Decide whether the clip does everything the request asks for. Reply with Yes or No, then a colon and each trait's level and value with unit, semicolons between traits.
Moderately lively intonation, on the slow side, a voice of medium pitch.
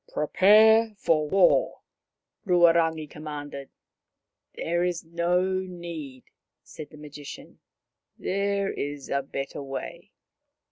Yes: average, 4.0 semitones; slow, 110 wpm; medium, 165 Hz